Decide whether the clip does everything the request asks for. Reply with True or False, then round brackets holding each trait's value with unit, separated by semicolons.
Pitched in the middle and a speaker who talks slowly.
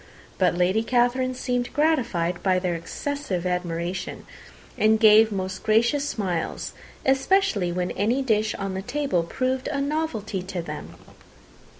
False (215 Hz; 130 wpm)